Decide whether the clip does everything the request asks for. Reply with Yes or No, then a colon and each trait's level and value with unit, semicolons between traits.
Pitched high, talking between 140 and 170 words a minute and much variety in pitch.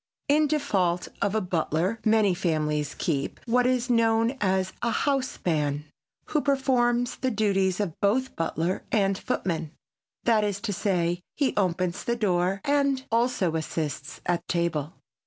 Yes: high, 200 Hz; average, 145 wpm; wide, 5.9 semitones